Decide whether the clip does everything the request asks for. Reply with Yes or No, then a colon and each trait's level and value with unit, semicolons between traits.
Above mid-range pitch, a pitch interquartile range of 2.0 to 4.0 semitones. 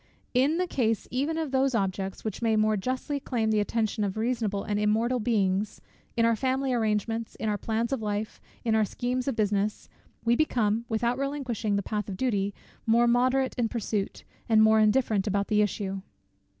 Yes: high, 225 Hz; average, 3.0 semitones